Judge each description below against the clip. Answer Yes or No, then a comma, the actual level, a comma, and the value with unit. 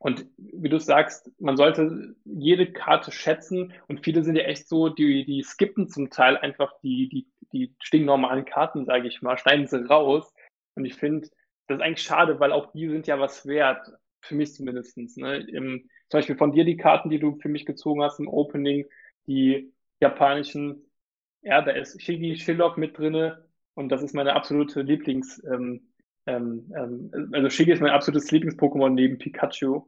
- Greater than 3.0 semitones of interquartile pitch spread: No, narrow, 2.5 semitones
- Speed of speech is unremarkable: Yes, average, 180 wpm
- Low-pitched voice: No, medium, 145 Hz